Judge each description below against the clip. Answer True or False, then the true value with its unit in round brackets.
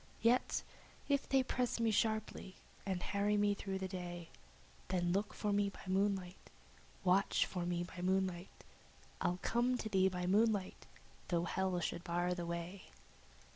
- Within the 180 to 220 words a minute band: False (155 wpm)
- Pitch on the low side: False (190 Hz)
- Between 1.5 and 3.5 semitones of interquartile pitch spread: True (2.6 semitones)